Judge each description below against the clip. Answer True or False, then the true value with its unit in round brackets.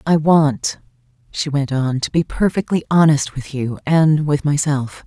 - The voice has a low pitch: False (145 Hz)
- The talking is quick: False (155 wpm)